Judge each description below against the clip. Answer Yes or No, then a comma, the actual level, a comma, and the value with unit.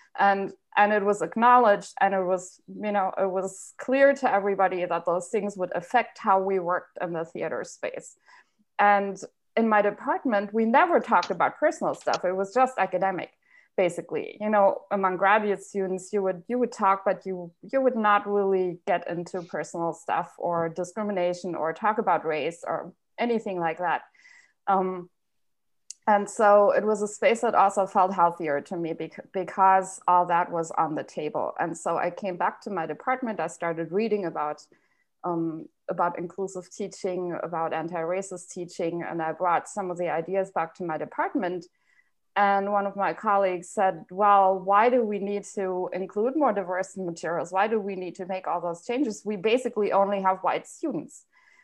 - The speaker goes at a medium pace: Yes, average, 180 wpm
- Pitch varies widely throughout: No, average, 2.8 semitones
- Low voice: No, high, 195 Hz